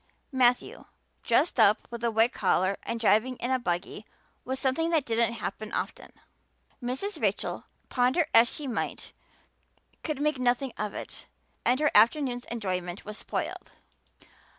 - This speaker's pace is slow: No, average, 145 wpm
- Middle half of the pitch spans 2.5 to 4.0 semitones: Yes, average, 3.3 semitones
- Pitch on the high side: Yes, high, 240 Hz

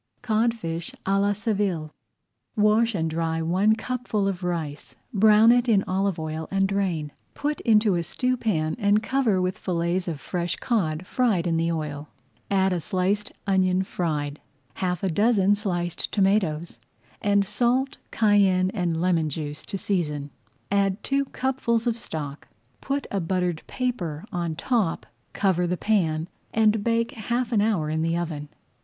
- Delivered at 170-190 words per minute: No, average, 150 wpm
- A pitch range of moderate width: Yes, average, 4.5 semitones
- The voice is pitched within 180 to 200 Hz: Yes, high, 190 Hz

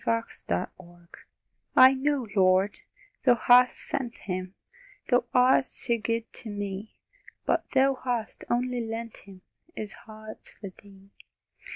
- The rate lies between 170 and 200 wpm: No, slow, 135 wpm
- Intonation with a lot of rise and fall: No, average, 4.0 semitones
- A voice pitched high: Yes, high, 225 Hz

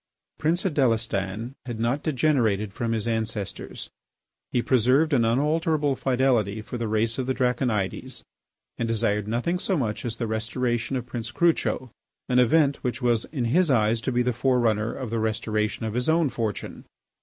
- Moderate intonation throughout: Yes, average, 3.2 semitones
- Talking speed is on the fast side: No, average, 170 wpm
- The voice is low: Yes, low, 120 Hz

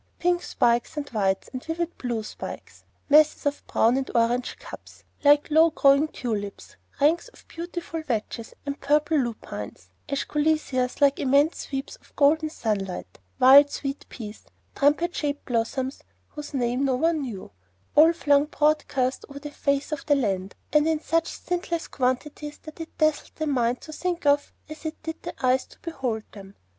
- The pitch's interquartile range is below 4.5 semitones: Yes, average, 3.8 semitones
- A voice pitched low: No, very high, 285 Hz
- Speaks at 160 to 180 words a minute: Yes, average, 165 wpm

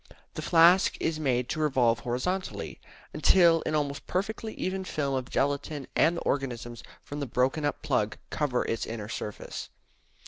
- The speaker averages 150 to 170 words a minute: Yes, average, 160 wpm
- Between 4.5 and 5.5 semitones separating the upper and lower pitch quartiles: Yes, average, 4.8 semitones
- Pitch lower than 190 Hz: Yes, medium, 140 Hz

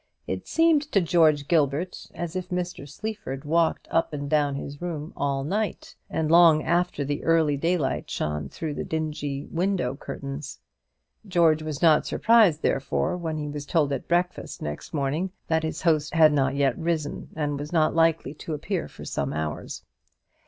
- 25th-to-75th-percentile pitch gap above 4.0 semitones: No, average, 3.2 semitones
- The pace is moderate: Yes, average, 170 wpm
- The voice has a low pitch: No, medium, 155 Hz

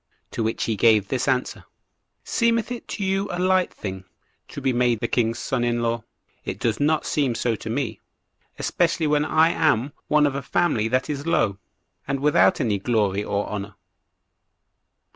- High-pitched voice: No, low, 125 Hz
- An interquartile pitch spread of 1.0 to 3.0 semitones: No, average, 5.2 semitones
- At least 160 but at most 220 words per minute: Yes, average, 175 wpm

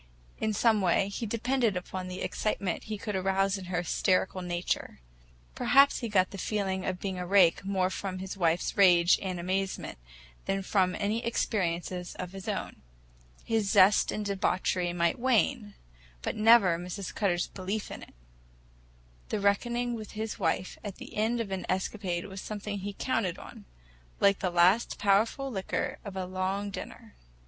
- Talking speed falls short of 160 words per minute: No, average, 165 wpm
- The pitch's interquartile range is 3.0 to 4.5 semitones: No, narrow, 2.5 semitones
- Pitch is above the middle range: Yes, high, 195 Hz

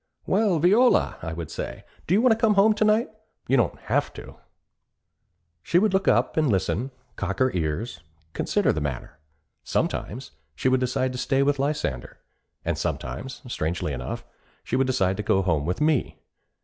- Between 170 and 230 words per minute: Yes, average, 175 wpm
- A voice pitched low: Yes, low, 130 Hz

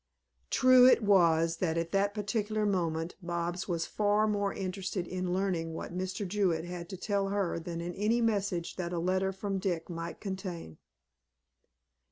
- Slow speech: No, average, 165 wpm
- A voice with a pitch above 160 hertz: Yes, medium, 185 Hz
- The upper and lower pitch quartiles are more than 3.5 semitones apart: No, average, 3.0 semitones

